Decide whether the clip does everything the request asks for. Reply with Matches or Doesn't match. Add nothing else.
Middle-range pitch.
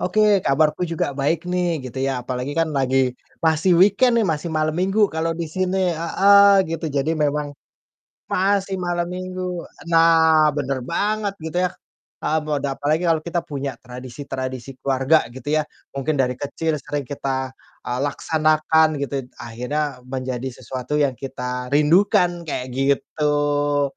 Matches